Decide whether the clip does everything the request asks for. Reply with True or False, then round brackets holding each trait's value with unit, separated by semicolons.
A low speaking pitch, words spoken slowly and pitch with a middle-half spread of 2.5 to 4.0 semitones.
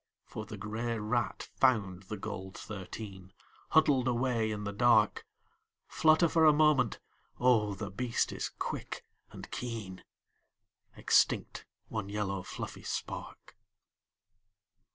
True (110 Hz; 115 wpm; 3.6 semitones)